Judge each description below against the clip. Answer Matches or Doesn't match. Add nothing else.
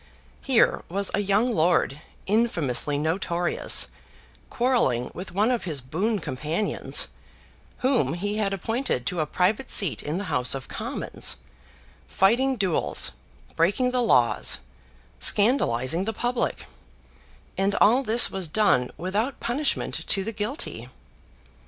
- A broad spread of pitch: Matches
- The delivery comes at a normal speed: Doesn't match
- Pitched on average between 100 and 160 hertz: Doesn't match